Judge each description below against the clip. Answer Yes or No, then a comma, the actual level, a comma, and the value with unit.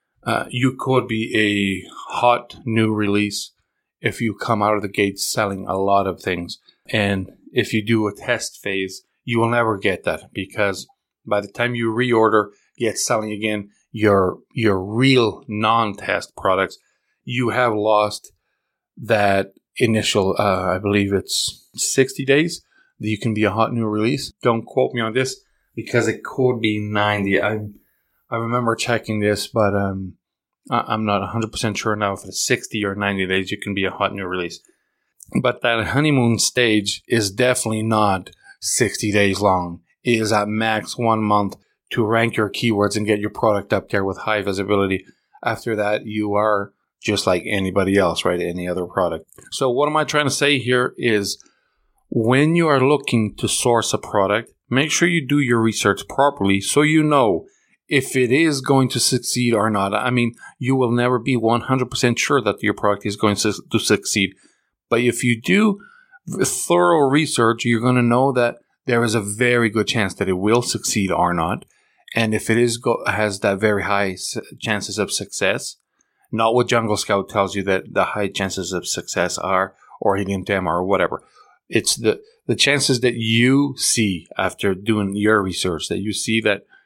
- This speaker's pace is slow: No, average, 180 wpm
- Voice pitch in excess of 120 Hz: No, low, 110 Hz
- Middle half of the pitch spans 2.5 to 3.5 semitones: Yes, average, 3.2 semitones